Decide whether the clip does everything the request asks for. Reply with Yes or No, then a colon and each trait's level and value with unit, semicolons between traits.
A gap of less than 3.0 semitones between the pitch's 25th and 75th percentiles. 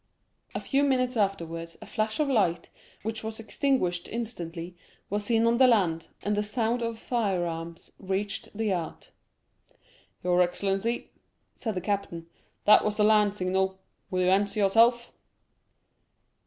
No: average, 3.8 semitones